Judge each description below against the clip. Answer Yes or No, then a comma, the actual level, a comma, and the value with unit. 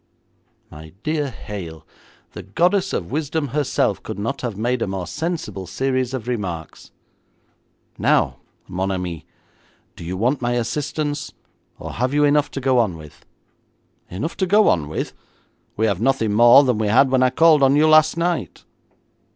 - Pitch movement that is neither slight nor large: No, wide, 7.1 semitones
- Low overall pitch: Yes, low, 125 Hz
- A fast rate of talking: No, average, 165 wpm